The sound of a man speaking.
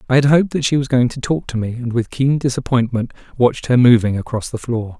Yes: male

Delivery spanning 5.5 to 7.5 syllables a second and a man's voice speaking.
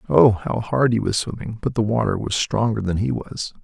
No: 5.1 syllables/s; male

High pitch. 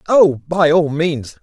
No: medium, 155 Hz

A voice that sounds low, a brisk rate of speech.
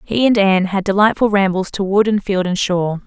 No: high, 195 Hz; fast, 235 wpm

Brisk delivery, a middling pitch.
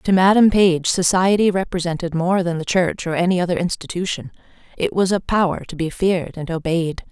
No: average, 185 wpm; medium, 180 Hz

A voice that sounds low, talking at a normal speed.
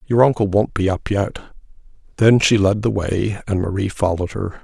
Yes: low, 100 Hz; average, 195 wpm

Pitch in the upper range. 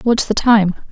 Yes: high, 215 Hz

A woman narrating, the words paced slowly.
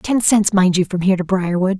No: female; fast, 270 wpm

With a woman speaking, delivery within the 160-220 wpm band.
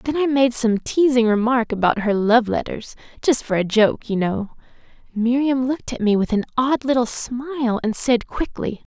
Yes: female; average, 180 wpm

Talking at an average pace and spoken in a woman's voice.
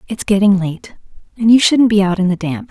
No: fast, 220 wpm; female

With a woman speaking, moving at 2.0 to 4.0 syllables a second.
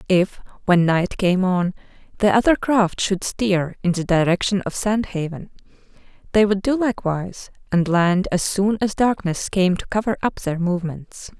No: female; 4.7 syllables/s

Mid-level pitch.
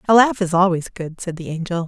Yes: medium, 180 Hz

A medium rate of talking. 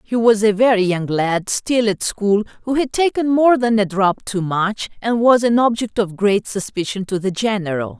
No: fast, 210 wpm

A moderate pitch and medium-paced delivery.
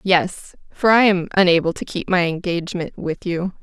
Yes: medium, 180 Hz; average, 180 wpm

